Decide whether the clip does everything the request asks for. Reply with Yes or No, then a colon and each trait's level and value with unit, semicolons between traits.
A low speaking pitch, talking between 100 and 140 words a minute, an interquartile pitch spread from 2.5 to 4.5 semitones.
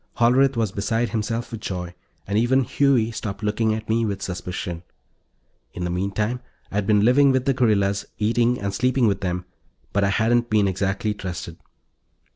No: low, 110 Hz; average, 170 wpm; average, 3.2 semitones